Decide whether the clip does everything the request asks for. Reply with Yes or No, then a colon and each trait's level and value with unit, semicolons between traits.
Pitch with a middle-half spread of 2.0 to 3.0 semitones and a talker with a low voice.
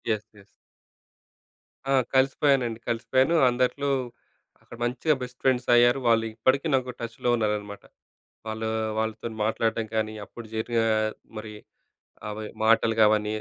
Yes: narrow, 2.4 semitones; low, 115 Hz